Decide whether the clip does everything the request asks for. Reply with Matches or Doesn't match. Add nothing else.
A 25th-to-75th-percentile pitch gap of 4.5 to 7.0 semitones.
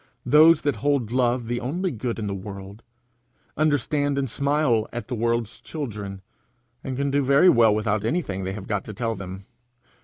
Matches